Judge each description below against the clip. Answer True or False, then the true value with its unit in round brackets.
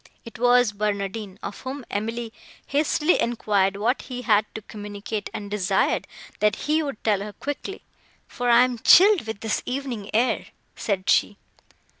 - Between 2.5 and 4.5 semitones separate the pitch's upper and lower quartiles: True (3.4 semitones)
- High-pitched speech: True (225 Hz)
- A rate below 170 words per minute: True (155 wpm)